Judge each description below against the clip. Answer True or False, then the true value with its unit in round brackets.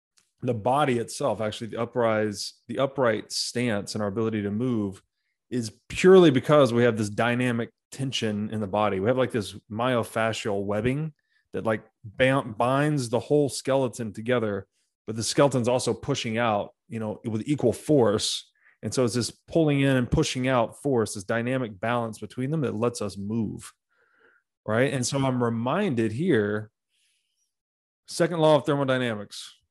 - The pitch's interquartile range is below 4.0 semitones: True (3.2 semitones)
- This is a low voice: True (120 Hz)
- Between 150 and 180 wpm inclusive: True (160 wpm)